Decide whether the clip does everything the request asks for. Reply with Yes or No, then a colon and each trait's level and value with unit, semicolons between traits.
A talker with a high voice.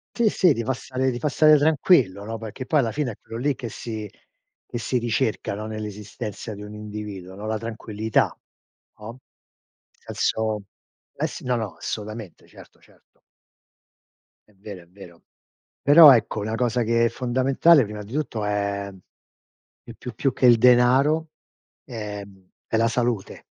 No: low, 115 Hz